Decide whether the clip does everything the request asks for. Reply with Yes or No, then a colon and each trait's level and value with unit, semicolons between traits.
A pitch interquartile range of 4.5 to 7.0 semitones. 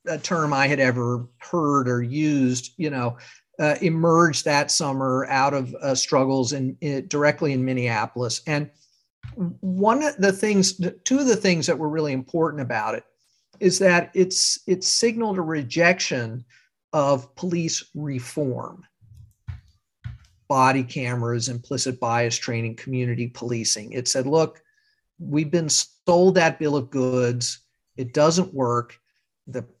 Yes: wide, 5.5 semitones